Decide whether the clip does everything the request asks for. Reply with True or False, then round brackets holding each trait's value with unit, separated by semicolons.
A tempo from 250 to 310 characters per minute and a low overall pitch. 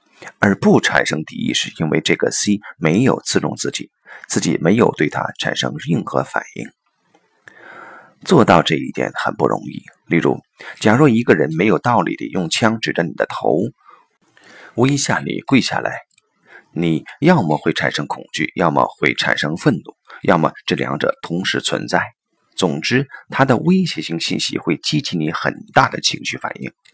False (240 characters per minute; 85 Hz)